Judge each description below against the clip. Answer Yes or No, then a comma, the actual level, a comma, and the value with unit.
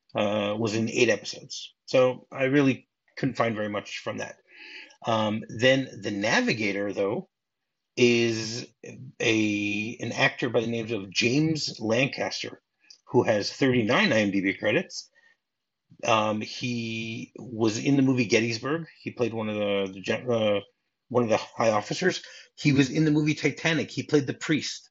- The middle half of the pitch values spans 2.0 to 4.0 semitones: No, average, 4.4 semitones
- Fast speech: No, average, 150 wpm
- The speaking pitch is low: Yes, low, 120 Hz